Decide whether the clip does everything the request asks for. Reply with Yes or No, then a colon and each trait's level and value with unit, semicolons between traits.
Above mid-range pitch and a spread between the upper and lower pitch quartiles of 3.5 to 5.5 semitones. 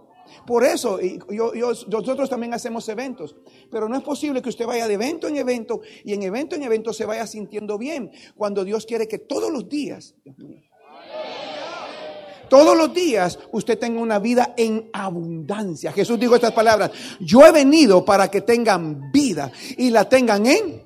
Yes: high, 230 Hz; average, 3.8 semitones